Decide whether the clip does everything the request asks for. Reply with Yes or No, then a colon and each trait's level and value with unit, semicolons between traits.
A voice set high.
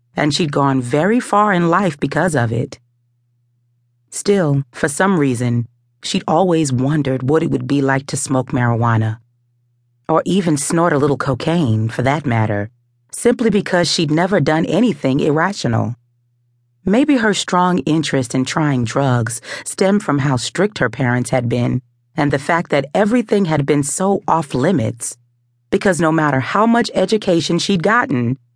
No: medium, 140 Hz